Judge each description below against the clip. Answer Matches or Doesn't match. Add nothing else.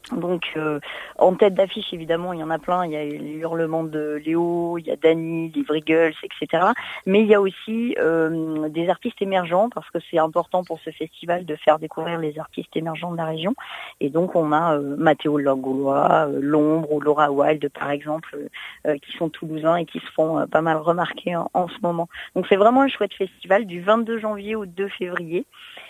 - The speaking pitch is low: Doesn't match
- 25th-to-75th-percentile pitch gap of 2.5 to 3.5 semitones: Matches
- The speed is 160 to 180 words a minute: Doesn't match